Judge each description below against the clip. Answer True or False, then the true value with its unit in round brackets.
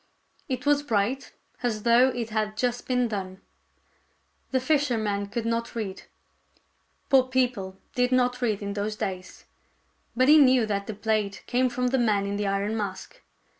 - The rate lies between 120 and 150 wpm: False (165 wpm)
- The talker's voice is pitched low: False (230 Hz)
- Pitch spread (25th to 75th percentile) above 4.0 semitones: False (3.7 semitones)